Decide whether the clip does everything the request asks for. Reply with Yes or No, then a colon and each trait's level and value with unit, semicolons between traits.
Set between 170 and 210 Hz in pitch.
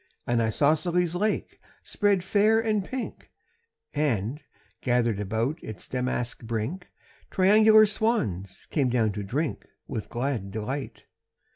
No: medium, 140 Hz